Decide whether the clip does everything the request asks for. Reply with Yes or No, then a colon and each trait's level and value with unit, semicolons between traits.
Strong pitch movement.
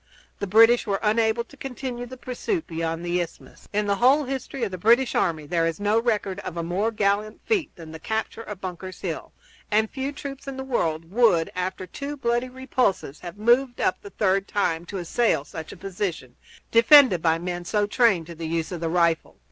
Yes: wide, 5.8 semitones